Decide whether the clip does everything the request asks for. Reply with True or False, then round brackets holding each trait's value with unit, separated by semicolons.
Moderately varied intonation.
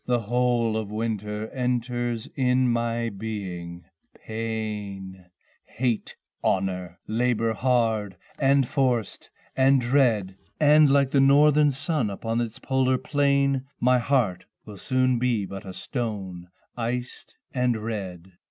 True (3.6 semitones)